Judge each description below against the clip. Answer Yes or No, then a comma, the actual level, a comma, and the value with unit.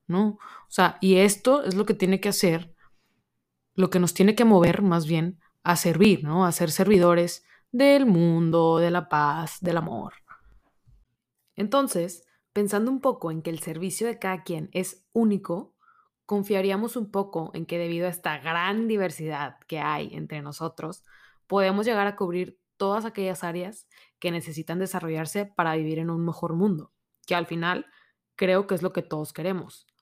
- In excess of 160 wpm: Yes, average, 170 wpm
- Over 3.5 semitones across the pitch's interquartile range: No, average, 3.2 semitones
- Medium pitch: Yes, medium, 180 Hz